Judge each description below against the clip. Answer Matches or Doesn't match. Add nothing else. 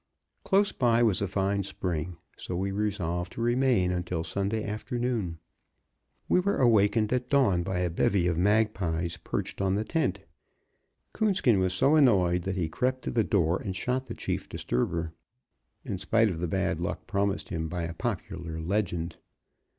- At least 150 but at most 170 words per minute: Matches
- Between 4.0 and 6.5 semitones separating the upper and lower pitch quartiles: Matches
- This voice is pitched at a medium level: Doesn't match